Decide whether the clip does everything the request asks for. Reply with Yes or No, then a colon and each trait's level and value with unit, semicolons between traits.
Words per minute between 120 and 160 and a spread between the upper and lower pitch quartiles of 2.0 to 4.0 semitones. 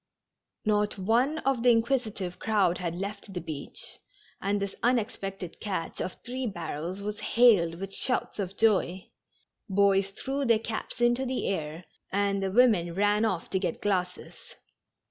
Yes: average, 150 wpm; average, 3.6 semitones